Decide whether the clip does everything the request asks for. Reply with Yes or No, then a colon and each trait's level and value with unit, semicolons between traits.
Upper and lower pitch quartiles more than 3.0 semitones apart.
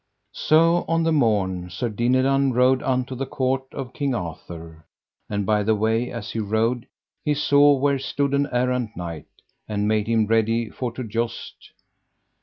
Yes: average, 4.0 semitones